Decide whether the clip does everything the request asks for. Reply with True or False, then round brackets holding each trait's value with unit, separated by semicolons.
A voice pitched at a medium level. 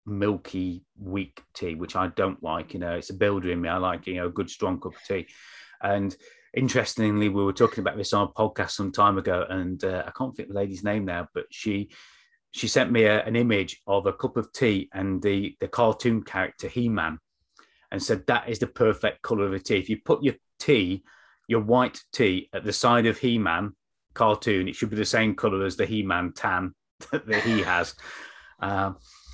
False (100 Hz)